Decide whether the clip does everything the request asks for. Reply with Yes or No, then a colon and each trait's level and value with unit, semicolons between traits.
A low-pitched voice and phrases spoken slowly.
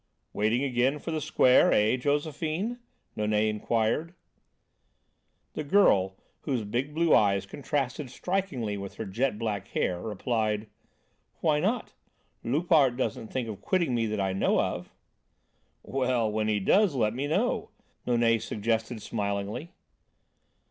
Yes: low, 120 Hz; slow, 130 wpm